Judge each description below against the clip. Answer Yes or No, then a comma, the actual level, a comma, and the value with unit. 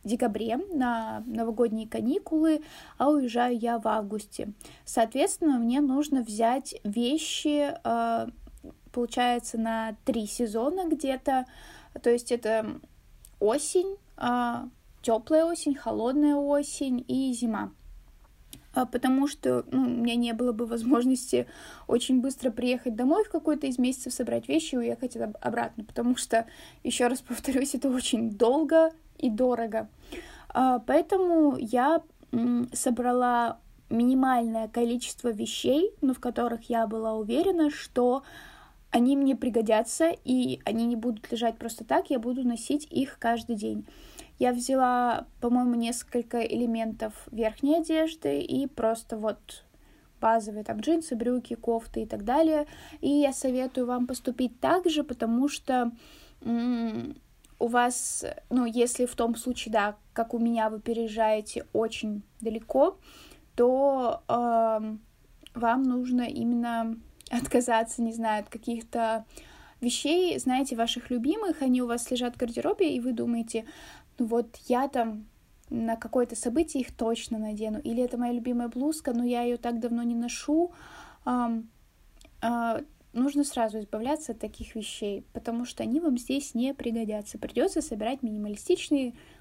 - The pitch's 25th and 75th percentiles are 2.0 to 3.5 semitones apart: Yes, average, 2.7 semitones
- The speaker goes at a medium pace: Yes, average, 130 wpm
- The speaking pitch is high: Yes, high, 245 Hz